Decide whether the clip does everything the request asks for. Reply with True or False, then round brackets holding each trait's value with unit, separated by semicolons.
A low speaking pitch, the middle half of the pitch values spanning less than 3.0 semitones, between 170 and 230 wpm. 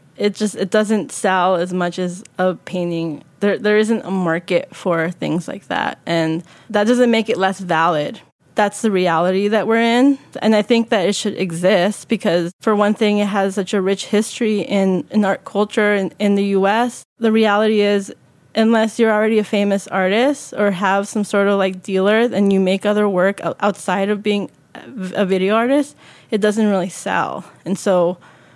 False (200 Hz; 2.5 semitones; 190 wpm)